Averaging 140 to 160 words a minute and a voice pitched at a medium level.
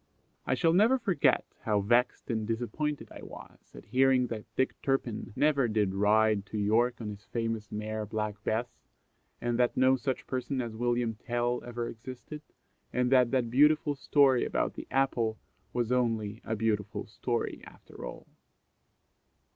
No: average, 155 wpm; low, 120 Hz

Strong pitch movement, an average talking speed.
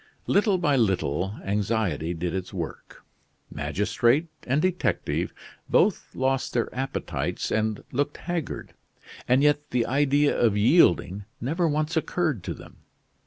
No: wide, 6.3 semitones; slow, 125 wpm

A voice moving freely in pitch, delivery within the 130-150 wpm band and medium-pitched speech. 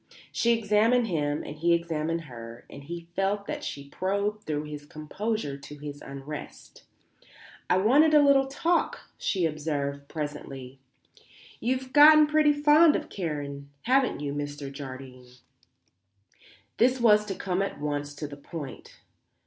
Yes: wide, 7.7 semitones; average, 140 wpm; medium, 160 Hz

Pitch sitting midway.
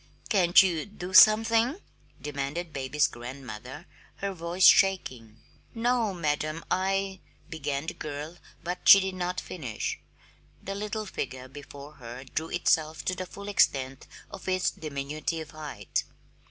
Yes: medium, 160 Hz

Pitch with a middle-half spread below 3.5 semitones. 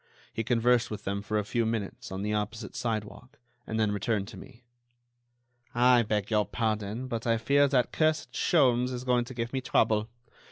Yes: average, 2.8 semitones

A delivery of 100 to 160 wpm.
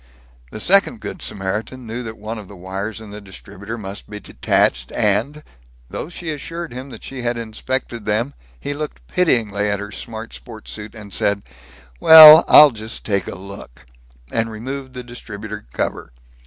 No: average, 170 wpm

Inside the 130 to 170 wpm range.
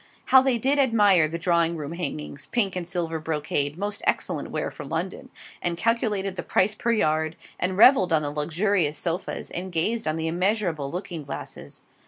No: average, 180 wpm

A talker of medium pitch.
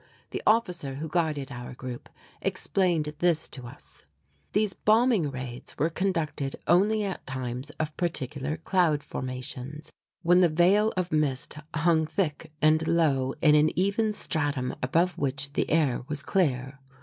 Yes: medium, 155 Hz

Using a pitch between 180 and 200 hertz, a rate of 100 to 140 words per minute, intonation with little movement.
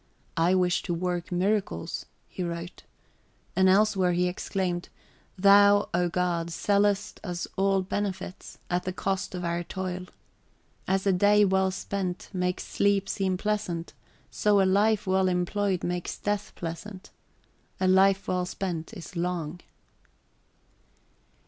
Yes: medium, 185 Hz; slow, 135 wpm; narrow, 1.9 semitones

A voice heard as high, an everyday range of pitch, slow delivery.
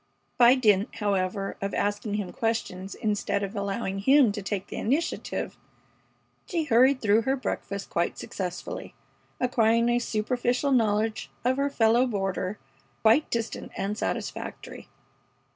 Yes: high, 220 Hz; average, 3.6 semitones; slow, 130 wpm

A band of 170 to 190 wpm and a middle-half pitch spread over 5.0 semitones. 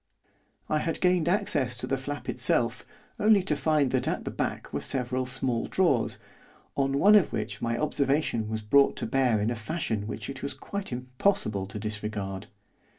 Yes: average, 180 wpm; wide, 5.4 semitones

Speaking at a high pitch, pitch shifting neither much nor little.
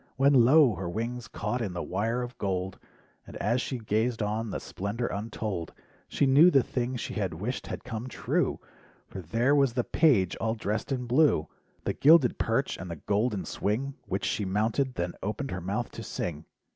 No: low, 115 Hz; average, 4.1 semitones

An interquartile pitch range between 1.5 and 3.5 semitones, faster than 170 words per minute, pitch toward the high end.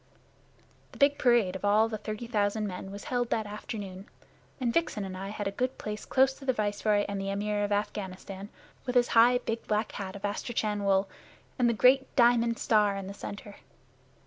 Yes: average, 2.9 semitones; average, 195 wpm; high, 210 Hz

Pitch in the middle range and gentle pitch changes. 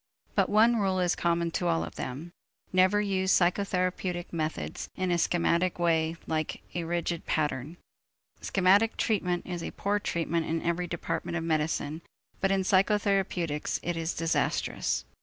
Yes: medium, 175 Hz; narrow, 2.3 semitones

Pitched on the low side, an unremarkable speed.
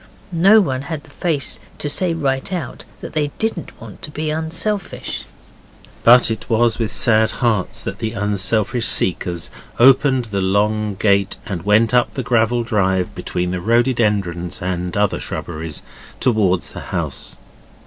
Yes: low, 115 Hz; average, 150 wpm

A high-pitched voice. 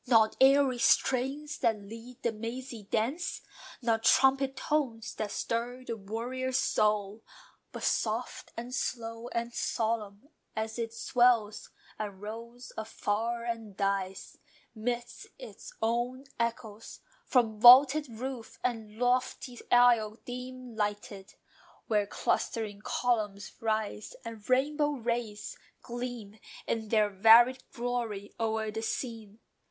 Yes: high, 230 Hz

